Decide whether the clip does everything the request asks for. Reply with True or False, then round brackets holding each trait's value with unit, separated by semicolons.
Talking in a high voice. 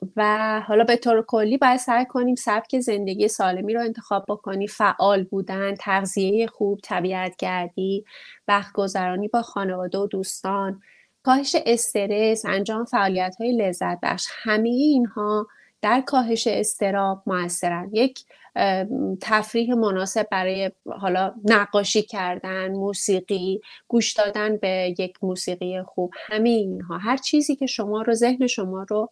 True (205 Hz)